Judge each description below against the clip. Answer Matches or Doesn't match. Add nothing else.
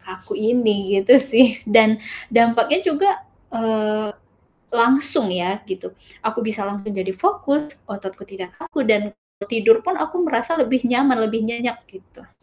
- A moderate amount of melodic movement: Matches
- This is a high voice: Matches